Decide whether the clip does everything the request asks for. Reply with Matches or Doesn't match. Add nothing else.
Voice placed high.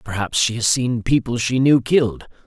Doesn't match